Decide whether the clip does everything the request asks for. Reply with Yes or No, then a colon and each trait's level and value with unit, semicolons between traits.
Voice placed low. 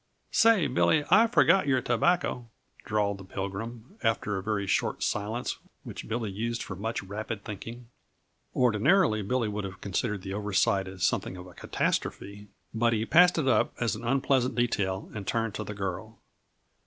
Yes: low, 110 Hz